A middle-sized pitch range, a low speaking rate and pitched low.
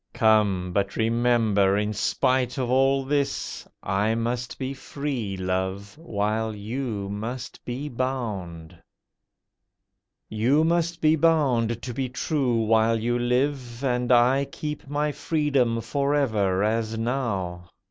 Yes: average, 4.2 semitones; slow, 125 wpm; low, 120 Hz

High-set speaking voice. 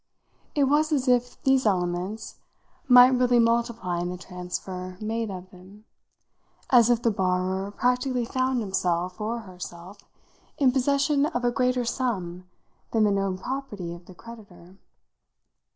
Yes: high, 220 Hz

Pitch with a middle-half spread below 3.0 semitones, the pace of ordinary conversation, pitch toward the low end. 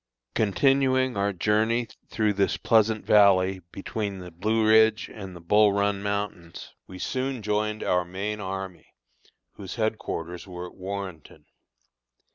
No: narrow, 2.6 semitones; slow, 130 wpm; low, 100 Hz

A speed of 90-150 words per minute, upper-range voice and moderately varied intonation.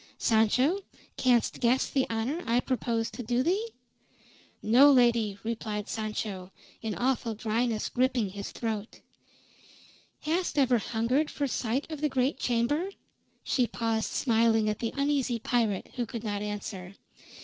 Yes: average, 140 wpm; high, 235 Hz; average, 3.0 semitones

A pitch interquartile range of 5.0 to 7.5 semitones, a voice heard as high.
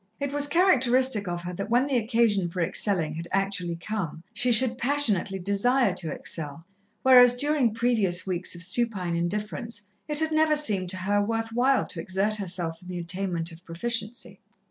Yes: wide, 5.6 semitones; high, 205 Hz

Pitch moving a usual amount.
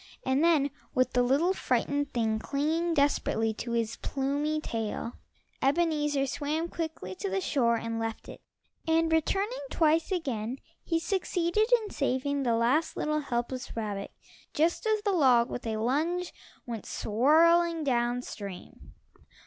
No: wide, 5.8 semitones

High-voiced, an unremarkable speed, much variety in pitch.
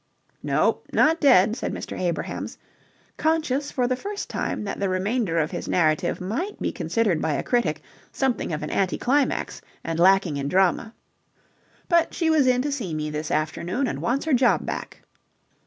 Yes: high, 215 Hz; average, 175 wpm; wide, 8.2 semitones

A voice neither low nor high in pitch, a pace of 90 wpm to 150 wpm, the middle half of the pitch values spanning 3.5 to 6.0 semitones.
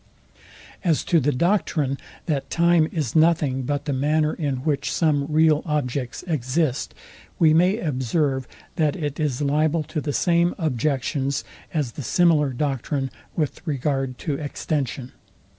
No: medium, 150 Hz; average, 140 wpm; average, 2.9 semitones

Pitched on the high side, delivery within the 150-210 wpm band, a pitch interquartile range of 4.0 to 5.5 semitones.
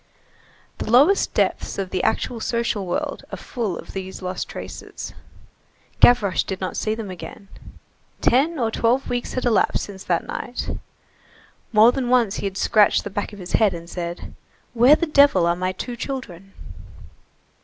Yes: high, 215 Hz; average, 165 wpm; average, 4.6 semitones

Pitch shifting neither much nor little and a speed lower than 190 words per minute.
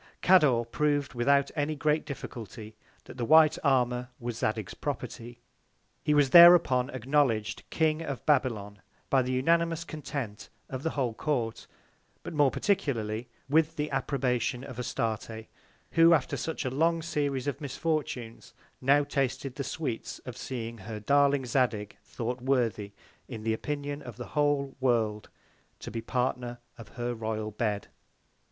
Yes: average, 4.0 semitones; average, 145 wpm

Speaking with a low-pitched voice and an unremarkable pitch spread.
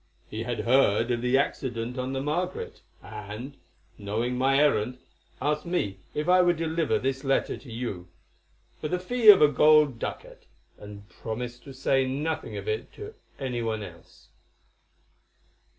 Yes: low, 130 Hz; average, 4.7 semitones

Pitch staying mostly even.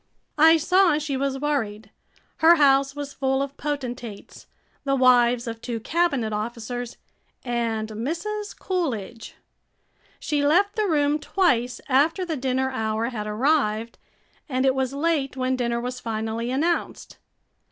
No: average, 4.1 semitones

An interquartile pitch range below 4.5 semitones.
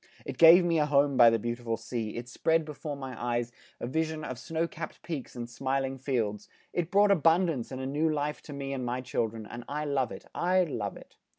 No: average, 4.8 semitones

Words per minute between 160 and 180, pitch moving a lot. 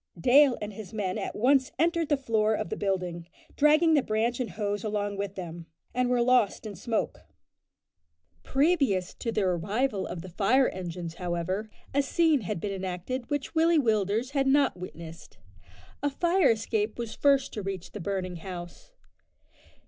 Yes: average, 170 wpm; wide, 6.2 semitones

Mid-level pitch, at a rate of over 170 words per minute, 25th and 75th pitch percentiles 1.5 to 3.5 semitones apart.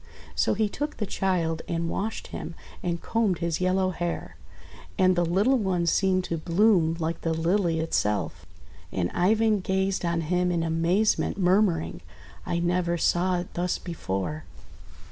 No: medium, 175 Hz; average, 150 wpm; narrow, 2.5 semitones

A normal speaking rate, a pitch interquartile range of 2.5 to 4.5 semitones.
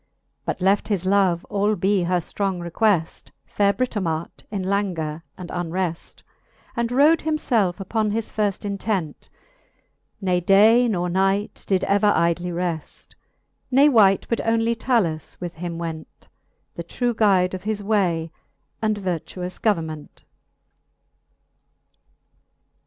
No: slow, 125 wpm; average, 3.5 semitones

